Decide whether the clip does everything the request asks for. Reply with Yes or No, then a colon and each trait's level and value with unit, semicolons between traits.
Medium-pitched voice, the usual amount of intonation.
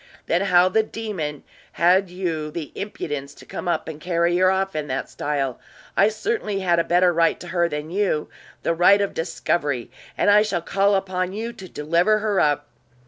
Yes: medium, 175 Hz; average, 3.7 semitones